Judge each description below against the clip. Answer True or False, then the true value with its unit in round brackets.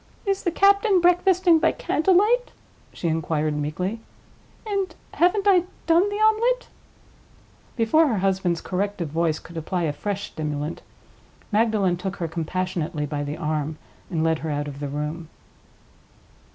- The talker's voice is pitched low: False (185 Hz)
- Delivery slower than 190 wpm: True (145 wpm)